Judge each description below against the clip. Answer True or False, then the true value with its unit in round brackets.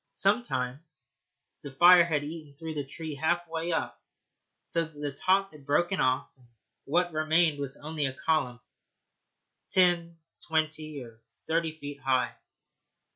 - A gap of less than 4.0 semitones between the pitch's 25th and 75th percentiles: True (2.9 semitones)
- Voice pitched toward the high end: False (155 Hz)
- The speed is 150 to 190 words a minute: False (135 wpm)